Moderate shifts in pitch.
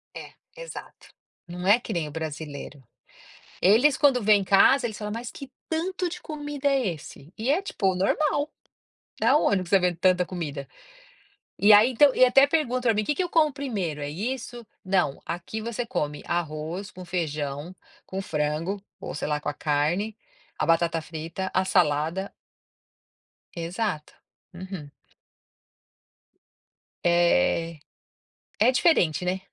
No: wide, 7.2 semitones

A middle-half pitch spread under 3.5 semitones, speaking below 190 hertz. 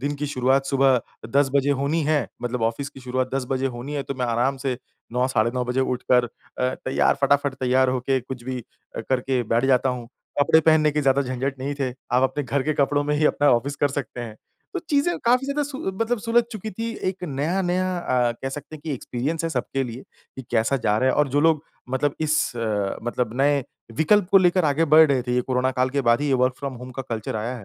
Yes: average, 3.0 semitones; low, 135 Hz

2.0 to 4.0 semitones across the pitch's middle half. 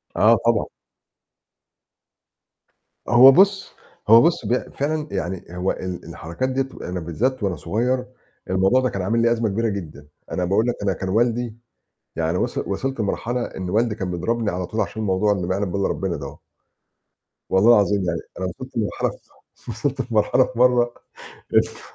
No: average, 4.7 semitones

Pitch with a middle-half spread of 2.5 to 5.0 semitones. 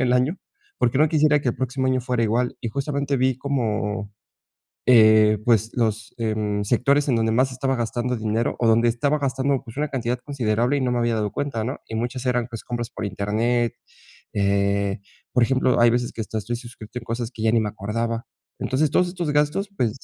Yes: average, 2.9 semitones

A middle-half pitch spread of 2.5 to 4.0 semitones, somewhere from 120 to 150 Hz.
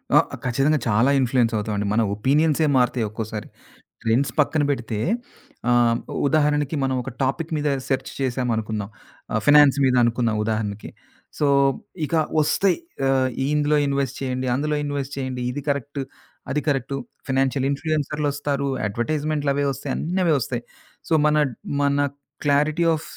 Yes: average, 3.3 semitones; low, 135 Hz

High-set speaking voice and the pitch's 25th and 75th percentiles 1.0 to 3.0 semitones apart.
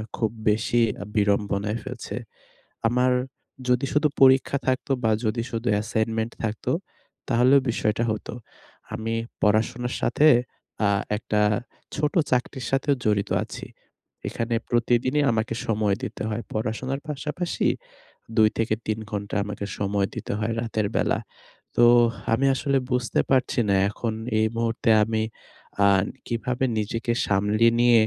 No: low, 115 Hz; narrow, 2.6 semitones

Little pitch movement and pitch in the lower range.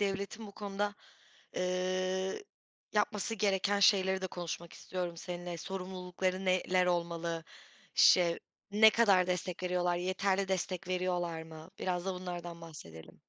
No: narrow, 1.7 semitones; medium, 185 Hz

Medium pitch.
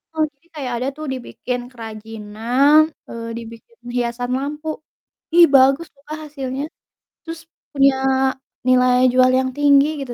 No: very high, 260 Hz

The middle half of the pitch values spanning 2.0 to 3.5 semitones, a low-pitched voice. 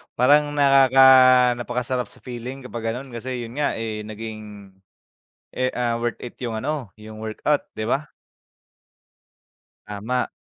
Yes: average, 2.7 semitones; low, 125 Hz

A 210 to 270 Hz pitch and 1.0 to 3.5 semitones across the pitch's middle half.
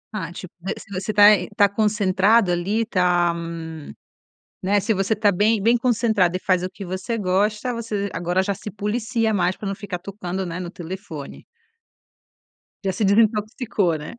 No: high, 200 Hz; average, 2.8 semitones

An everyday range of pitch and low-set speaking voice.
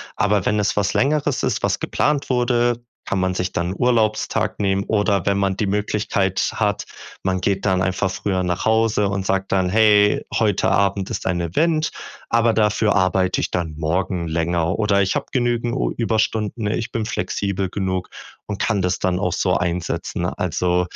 Yes: average, 3.0 semitones; low, 100 Hz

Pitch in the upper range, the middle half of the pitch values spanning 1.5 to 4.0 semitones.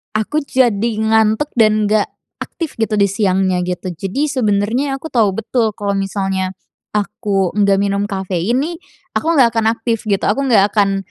Yes: high, 210 Hz; average, 3.0 semitones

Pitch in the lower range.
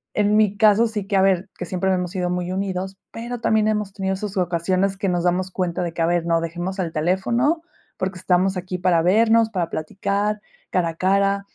No: high, 190 Hz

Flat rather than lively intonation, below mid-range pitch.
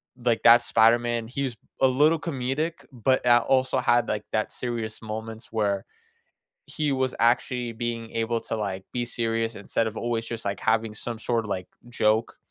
Yes: narrow, 1.9 semitones; low, 115 Hz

